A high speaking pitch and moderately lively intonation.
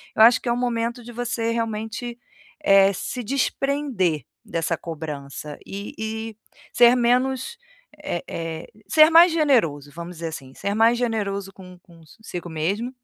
No: high, 220 Hz; wide, 6.2 semitones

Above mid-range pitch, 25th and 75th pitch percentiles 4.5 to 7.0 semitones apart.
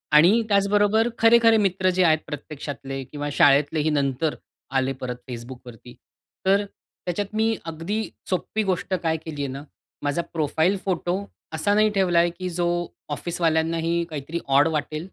No: medium, 165 Hz; average, 4.9 semitones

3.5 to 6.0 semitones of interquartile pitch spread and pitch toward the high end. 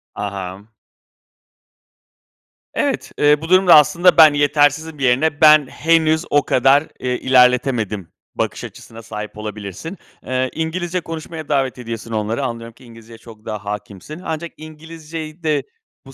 No: wide, 5.6 semitones; medium, 140 Hz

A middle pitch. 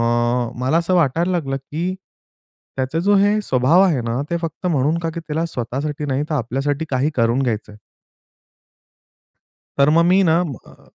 Yes: medium, 145 Hz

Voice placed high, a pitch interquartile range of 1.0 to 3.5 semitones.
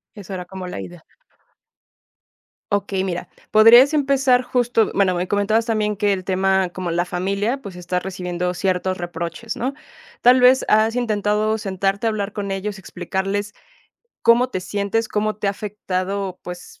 Yes: high, 200 Hz; average, 2.9 semitones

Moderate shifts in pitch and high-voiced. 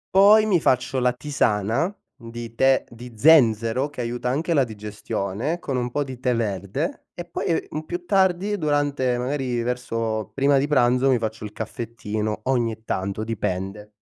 No: average, 4.6 semitones; low, 125 Hz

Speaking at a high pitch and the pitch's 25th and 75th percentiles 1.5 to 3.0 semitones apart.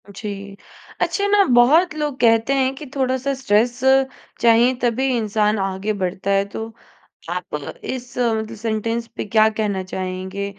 No: high, 225 Hz; average, 3.9 semitones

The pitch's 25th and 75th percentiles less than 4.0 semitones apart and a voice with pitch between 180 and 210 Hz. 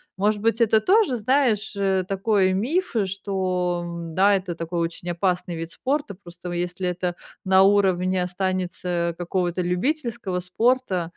Yes: average, 2.8 semitones; medium, 185 Hz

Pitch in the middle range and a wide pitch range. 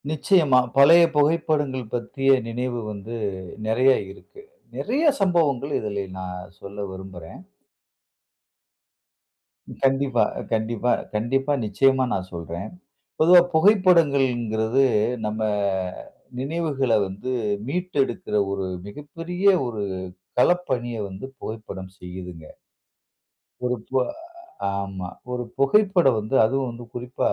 No: low, 125 Hz; wide, 5.7 semitones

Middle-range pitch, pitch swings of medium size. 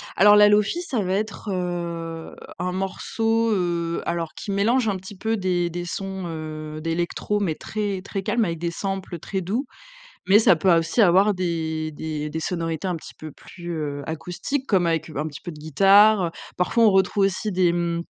Yes: medium, 180 Hz; average, 3.5 semitones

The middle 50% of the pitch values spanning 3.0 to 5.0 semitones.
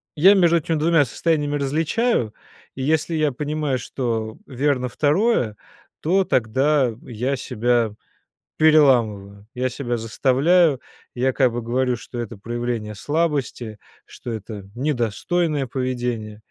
Yes: average, 4.4 semitones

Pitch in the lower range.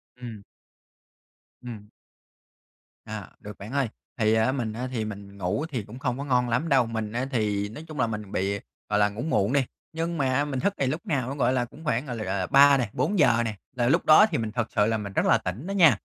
Yes: low, 120 Hz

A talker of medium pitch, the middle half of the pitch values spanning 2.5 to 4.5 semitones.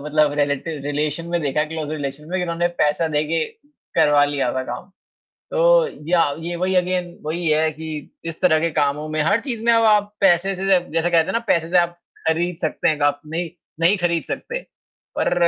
Yes: medium, 165 Hz; average, 2.8 semitones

